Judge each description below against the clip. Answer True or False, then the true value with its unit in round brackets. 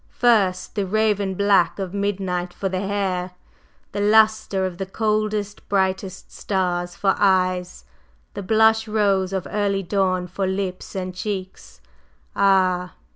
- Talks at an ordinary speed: False (130 wpm)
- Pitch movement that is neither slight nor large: False (1.8 semitones)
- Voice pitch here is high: True (195 Hz)